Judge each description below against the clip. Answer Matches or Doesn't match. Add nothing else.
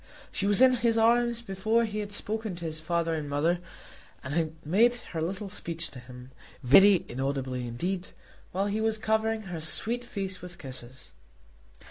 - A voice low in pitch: Doesn't match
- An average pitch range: Doesn't match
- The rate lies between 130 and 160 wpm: Doesn't match